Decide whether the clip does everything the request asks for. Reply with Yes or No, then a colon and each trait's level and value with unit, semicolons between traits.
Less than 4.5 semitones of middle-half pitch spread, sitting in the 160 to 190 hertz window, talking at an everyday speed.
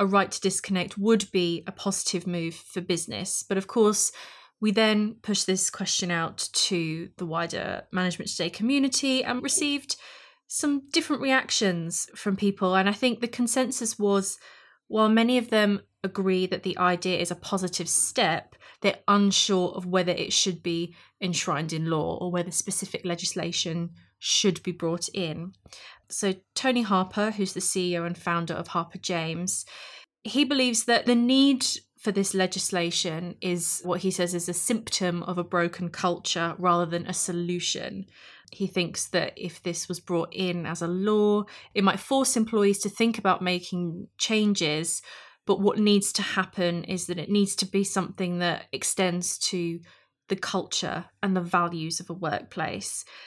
Yes: average, 2.9 semitones; medium, 185 Hz; average, 165 wpm